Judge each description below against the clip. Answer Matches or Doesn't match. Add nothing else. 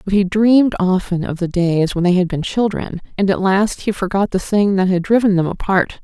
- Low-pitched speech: Doesn't match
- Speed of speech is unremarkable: Doesn't match